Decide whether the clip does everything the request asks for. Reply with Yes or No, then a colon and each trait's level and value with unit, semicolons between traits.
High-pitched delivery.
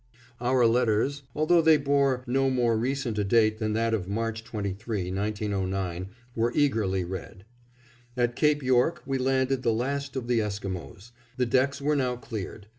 No: low, 120 Hz